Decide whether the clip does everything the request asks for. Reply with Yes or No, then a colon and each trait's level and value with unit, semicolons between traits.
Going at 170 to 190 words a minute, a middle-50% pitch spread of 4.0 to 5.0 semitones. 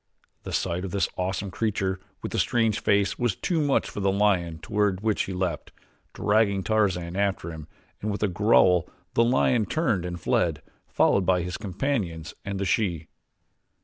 No: average, 175 wpm; average, 3.1 semitones